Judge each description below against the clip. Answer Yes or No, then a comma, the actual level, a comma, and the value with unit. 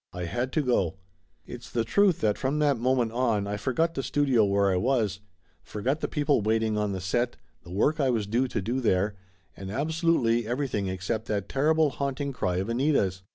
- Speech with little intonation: No, average, 5.1 semitones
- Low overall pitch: Yes, low, 120 Hz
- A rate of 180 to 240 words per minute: Yes, average, 200 wpm